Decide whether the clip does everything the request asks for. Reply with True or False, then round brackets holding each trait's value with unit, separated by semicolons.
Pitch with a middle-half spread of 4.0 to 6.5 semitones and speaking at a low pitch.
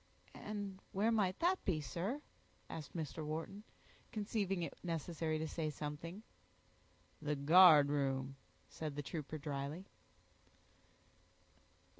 False (4.6 semitones; 160 Hz)